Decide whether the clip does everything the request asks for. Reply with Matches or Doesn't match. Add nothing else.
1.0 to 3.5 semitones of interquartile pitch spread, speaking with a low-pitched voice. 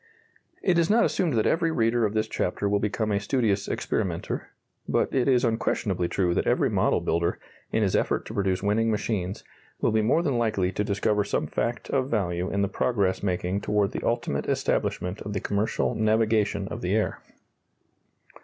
Matches